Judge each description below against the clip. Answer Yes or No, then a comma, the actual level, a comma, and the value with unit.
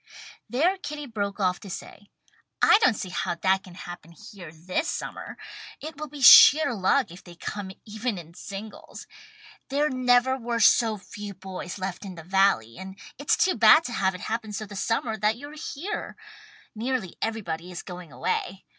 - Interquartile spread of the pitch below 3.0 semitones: No, average, 5.2 semitones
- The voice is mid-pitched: No, high, 205 Hz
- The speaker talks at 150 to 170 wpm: No, average, 180 wpm